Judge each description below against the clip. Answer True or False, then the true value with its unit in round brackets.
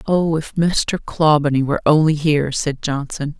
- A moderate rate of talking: True (160 wpm)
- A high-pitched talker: False (150 Hz)